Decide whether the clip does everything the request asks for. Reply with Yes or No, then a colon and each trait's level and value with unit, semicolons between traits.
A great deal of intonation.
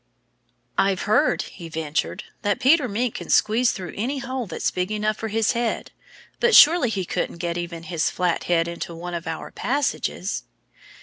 Yes: wide, 5.9 semitones